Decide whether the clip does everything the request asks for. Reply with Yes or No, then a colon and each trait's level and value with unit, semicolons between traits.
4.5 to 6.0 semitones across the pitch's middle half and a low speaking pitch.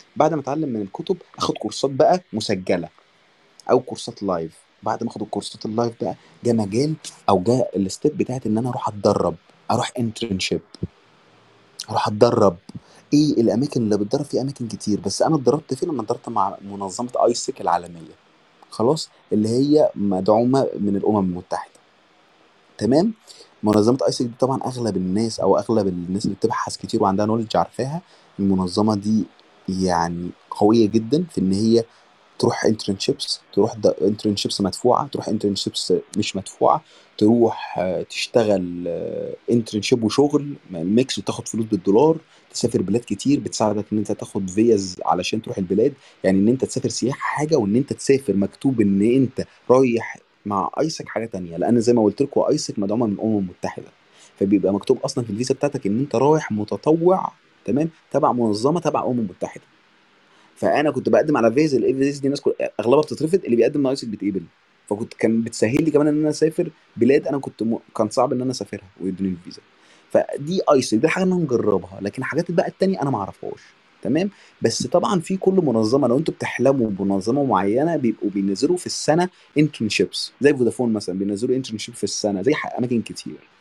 Yes: average, 5.1 semitones; low, 110 Hz